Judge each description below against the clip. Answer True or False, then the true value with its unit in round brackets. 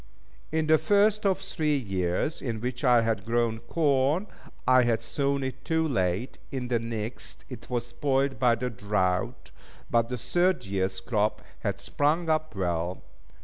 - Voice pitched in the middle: False (120 Hz)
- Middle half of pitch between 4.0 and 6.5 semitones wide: True (5.4 semitones)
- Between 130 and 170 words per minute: True (165 wpm)